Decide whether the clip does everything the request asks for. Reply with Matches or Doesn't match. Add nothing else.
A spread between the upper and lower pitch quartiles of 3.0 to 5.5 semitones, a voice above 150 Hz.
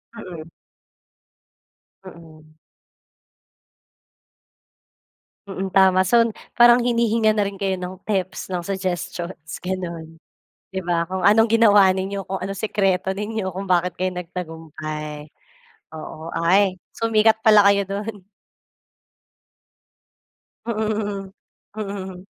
Doesn't match